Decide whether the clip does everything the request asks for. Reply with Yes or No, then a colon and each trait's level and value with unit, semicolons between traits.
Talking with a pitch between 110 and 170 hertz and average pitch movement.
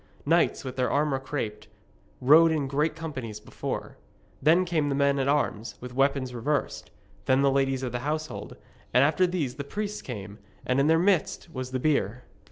Yes: medium, 140 Hz; average, 3.4 semitones